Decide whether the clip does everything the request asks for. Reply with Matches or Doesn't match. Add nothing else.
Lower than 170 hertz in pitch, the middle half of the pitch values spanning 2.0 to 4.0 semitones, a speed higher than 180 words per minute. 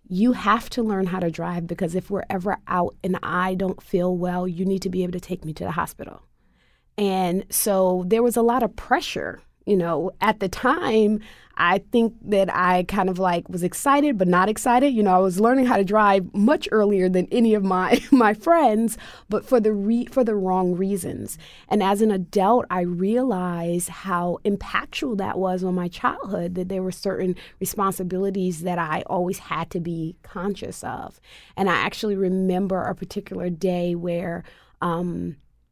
Doesn't match